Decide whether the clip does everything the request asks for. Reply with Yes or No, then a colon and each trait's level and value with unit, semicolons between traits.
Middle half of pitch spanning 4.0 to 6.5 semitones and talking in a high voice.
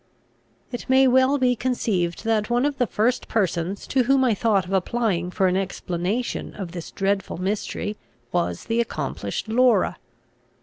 Yes: average, 5.2 semitones; high, 215 Hz